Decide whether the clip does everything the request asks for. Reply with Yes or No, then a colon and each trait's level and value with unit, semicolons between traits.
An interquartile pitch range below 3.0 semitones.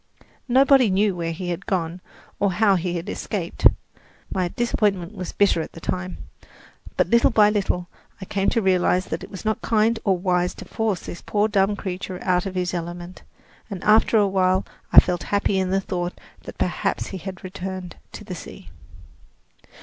Yes: narrow, 2.4 semitones